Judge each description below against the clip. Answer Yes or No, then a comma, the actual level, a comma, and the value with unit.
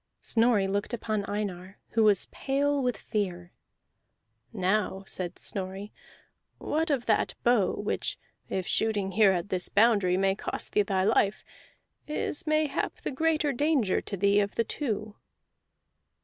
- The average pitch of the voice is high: Yes, high, 210 Hz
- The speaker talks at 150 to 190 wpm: No, average, 140 wpm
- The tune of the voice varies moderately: Yes, average, 4.0 semitones